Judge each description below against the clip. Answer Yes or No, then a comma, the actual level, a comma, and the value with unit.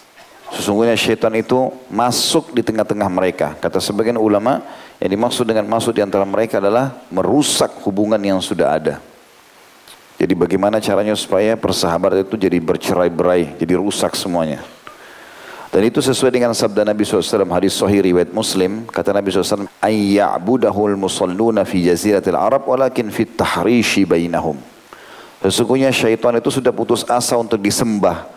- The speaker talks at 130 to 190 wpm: Yes, average, 135 wpm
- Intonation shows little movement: No, average, 3.3 semitones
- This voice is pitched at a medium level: No, low, 105 Hz